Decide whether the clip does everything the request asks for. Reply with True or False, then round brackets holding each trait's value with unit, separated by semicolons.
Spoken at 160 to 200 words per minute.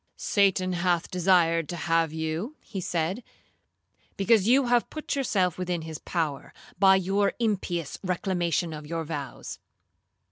False (135 wpm)